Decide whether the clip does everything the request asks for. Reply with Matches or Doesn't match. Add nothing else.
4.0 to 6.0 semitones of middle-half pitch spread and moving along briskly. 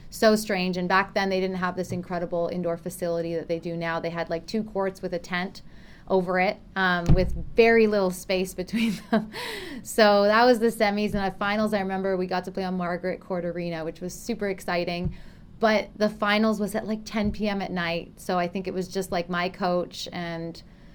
Doesn't match